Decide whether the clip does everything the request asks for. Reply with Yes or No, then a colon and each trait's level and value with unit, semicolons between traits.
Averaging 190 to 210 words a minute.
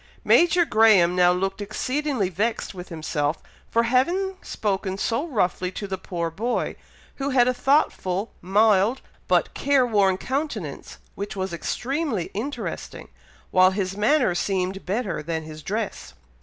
No: average, 140 wpm